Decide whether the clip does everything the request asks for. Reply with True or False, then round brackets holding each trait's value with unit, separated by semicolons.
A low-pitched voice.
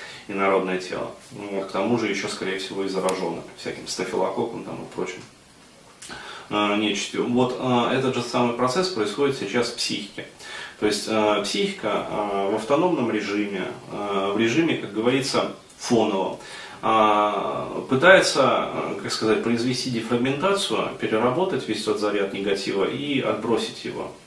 True (105 Hz)